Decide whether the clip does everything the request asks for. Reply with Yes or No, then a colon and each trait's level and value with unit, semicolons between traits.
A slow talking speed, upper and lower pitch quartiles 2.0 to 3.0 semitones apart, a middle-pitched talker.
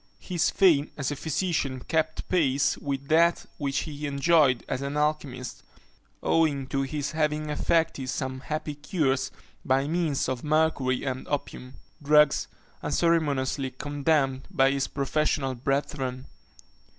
Yes: slow, 125 wpm; narrow, 2.6 semitones; medium, 145 Hz